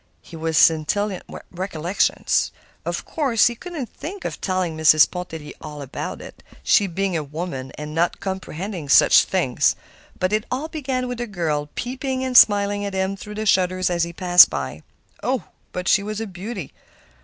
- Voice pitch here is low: No, medium, 185 Hz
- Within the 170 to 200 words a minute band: Yes, average, 180 wpm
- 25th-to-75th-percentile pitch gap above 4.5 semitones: Yes, average, 4.9 semitones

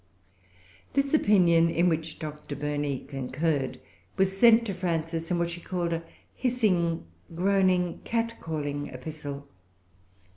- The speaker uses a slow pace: Yes, slow, 115 wpm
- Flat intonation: No, average, 4.2 semitones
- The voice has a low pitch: No, medium, 170 Hz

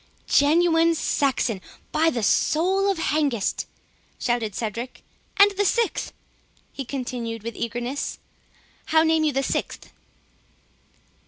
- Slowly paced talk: Yes, slow, 100 wpm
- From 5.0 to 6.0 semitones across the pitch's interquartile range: Yes, wide, 5.4 semitones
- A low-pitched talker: No, very high, 285 Hz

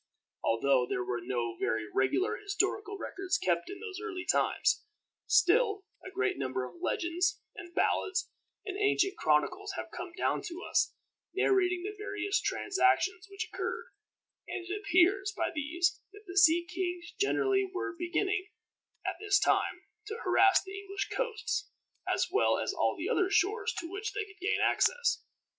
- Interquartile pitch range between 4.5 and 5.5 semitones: No, narrow, 2.6 semitones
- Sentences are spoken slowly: No, average, 160 wpm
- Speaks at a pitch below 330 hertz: No, very high, 385 Hz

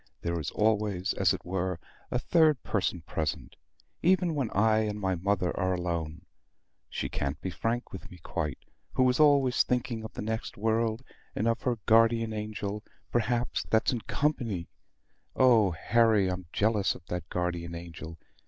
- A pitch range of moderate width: Yes, average, 4.6 semitones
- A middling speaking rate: Yes, average, 160 wpm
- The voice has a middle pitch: No, low, 105 Hz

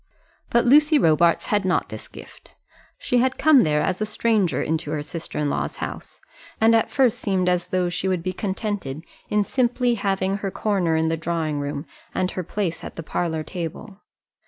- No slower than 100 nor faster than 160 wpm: No, average, 190 wpm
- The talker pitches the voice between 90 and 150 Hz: No, medium, 185 Hz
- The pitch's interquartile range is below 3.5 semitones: No, average, 4.7 semitones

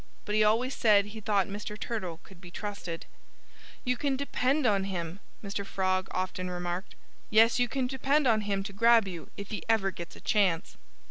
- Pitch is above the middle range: Yes, high, 205 Hz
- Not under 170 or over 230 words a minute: Yes, average, 190 wpm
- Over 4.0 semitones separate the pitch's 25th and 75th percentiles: No, average, 3.5 semitones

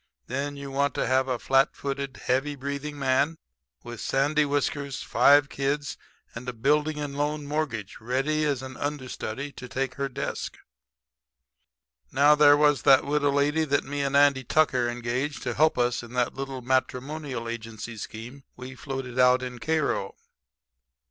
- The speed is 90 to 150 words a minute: No, average, 160 wpm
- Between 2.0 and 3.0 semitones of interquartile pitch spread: Yes, narrow, 2.4 semitones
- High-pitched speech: No, low, 135 Hz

